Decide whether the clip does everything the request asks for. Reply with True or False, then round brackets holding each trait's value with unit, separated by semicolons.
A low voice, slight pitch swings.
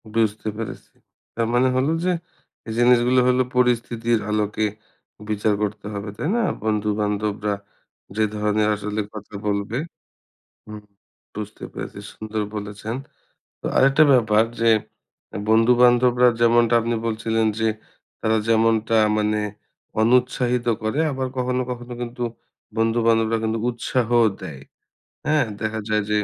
True (115 Hz; 2.3 semitones)